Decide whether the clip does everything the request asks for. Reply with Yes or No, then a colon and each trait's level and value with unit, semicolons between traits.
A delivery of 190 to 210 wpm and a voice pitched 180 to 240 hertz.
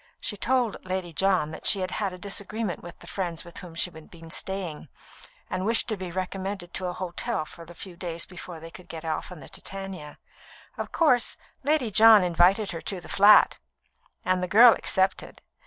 Yes: average, 200 wpm; medium, 185 Hz